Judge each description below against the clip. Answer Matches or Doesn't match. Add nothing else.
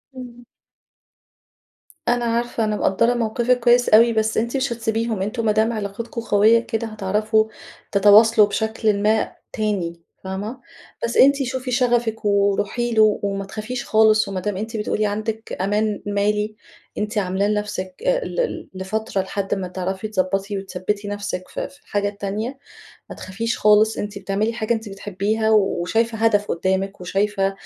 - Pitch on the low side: Doesn't match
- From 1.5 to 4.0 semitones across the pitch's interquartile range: Matches